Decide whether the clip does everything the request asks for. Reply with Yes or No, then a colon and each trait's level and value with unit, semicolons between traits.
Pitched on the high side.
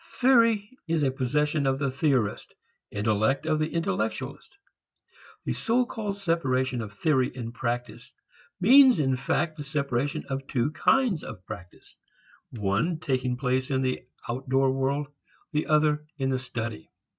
No: low, 135 Hz